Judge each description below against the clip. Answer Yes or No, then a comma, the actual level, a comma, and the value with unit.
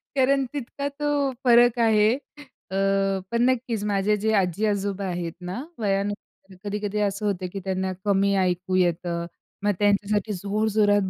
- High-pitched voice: Yes, high, 205 Hz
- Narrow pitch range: Yes, narrow, 2.3 semitones